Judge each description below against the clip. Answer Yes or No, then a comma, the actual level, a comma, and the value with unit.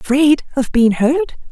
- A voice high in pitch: Yes, very high, 270 Hz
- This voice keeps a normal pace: Yes, average, 160 wpm